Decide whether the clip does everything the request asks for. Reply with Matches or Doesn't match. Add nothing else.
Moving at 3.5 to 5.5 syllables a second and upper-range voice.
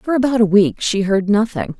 Matches